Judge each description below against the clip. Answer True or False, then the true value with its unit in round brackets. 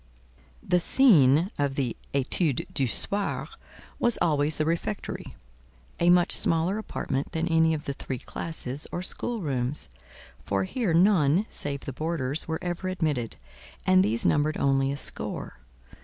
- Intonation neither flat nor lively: True (4.4 semitones)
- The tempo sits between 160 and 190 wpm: False (140 wpm)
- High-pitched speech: False (155 Hz)